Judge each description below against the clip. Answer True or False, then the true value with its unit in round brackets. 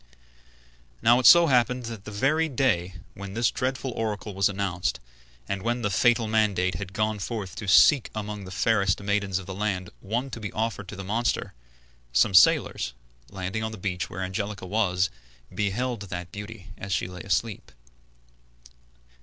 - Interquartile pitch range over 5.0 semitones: False (3.3 semitones)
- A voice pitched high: False (105 Hz)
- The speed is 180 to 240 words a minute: False (170 wpm)